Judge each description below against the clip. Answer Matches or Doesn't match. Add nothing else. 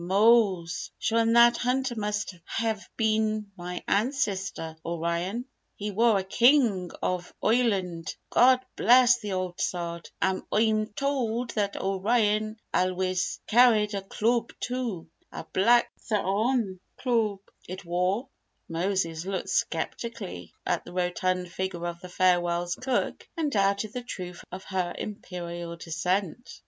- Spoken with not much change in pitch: Doesn't match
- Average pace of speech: Doesn't match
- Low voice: Doesn't match